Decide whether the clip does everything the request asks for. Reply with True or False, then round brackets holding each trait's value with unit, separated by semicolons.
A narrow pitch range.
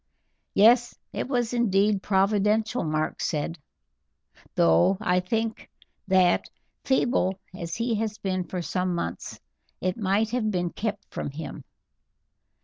False (3.7 semitones)